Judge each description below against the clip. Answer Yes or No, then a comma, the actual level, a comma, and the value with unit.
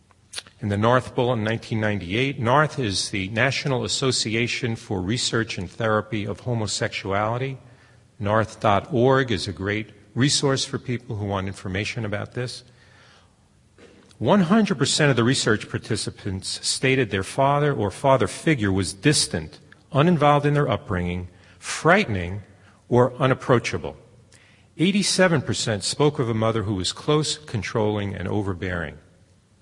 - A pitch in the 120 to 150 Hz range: No, low, 110 Hz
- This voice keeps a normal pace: No, slow, 120 wpm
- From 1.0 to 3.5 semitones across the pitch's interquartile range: No, average, 4.6 semitones